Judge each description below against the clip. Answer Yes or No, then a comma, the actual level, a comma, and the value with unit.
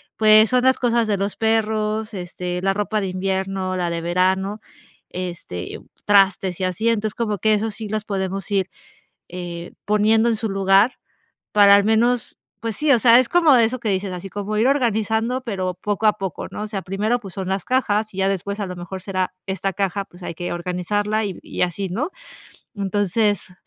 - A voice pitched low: No, high, 200 Hz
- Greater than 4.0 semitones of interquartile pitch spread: No, average, 2.8 semitones